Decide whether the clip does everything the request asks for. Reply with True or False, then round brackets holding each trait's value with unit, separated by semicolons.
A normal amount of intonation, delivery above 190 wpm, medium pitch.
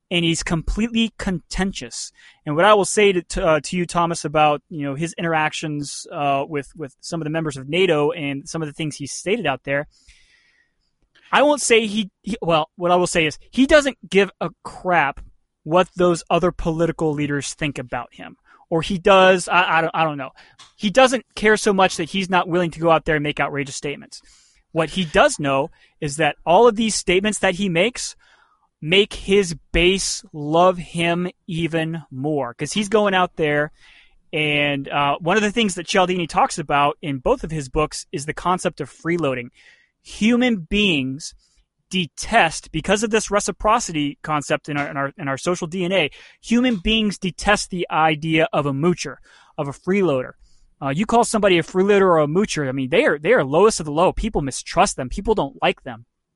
True (4.7 semitones; 200 wpm; 170 Hz)